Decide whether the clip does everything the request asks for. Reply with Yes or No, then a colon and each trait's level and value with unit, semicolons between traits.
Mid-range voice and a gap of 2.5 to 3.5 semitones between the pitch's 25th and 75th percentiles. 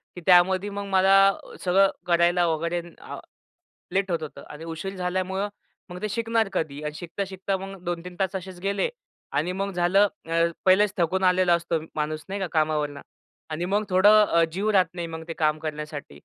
Yes: medium, 180 Hz; average, 2.8 semitones